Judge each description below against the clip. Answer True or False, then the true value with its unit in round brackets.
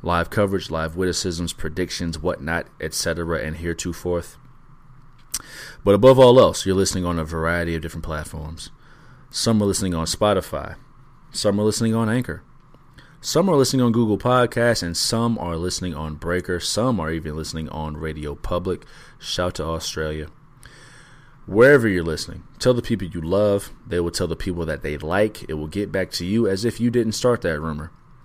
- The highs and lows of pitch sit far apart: True (6.0 semitones)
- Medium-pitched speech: False (90 Hz)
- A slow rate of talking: False (175 wpm)